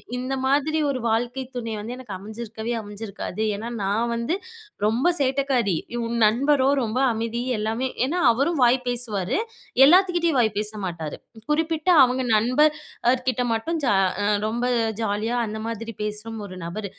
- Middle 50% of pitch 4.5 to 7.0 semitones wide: No, average, 3.6 semitones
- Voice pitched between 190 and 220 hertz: No, high, 235 Hz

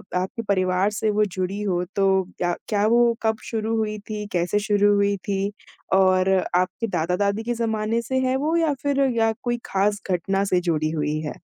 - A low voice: No, high, 205 Hz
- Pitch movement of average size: Yes, average, 3.1 semitones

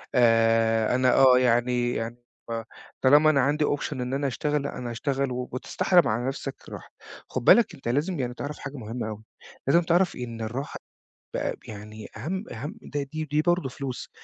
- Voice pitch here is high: No, low, 130 Hz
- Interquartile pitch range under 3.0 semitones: No, average, 3.8 semitones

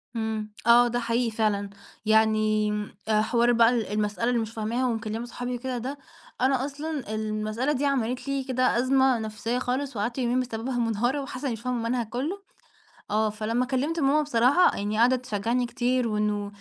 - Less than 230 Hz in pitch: No, high, 240 Hz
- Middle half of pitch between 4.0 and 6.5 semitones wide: No, average, 2.8 semitones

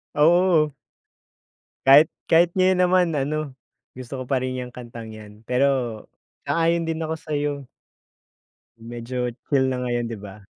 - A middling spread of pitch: Yes, average, 4.7 semitones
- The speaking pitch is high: No, medium, 140 Hz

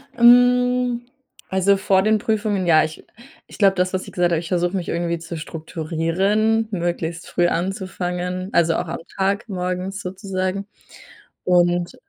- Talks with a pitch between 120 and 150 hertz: No, medium, 185 Hz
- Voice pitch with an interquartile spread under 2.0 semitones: No, narrow, 2.6 semitones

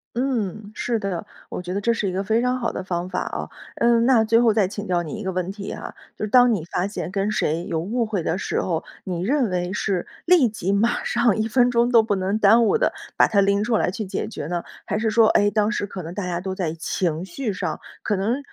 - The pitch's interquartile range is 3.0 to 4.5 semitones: Yes, average, 3.8 semitones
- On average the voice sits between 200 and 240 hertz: Yes, high, 205 Hz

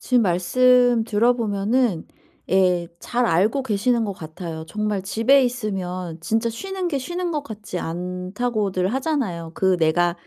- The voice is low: No, high, 210 Hz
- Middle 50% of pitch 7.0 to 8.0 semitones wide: No, wide, 5.4 semitones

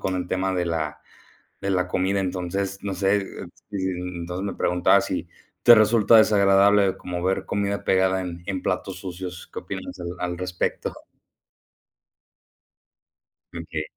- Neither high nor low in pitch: No, very low, 95 Hz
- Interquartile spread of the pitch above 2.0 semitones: No, narrow, 1.7 semitones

